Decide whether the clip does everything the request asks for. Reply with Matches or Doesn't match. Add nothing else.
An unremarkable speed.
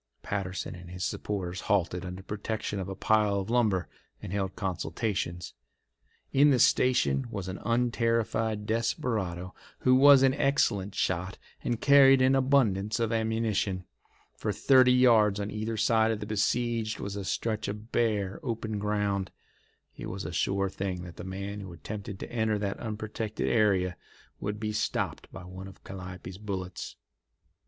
Matches